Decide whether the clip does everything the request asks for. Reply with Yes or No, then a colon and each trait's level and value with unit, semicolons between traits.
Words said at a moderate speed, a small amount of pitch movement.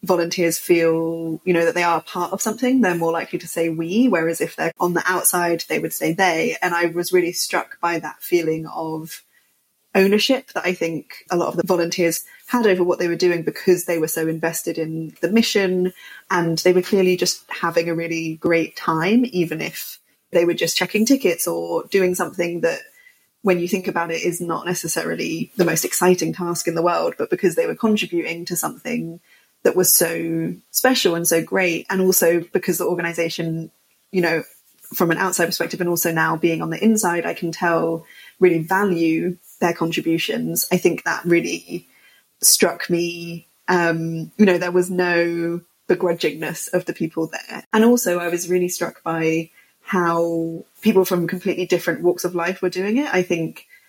Yes: average, 190 wpm; narrow, 1.7 semitones